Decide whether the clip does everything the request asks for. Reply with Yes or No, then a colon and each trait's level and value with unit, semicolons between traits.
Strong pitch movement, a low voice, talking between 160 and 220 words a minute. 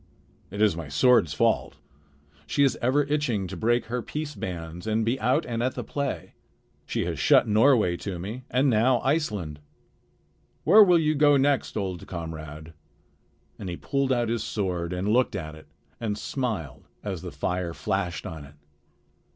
Yes: wide, 7.0 semitones; low, 110 Hz; average, 170 wpm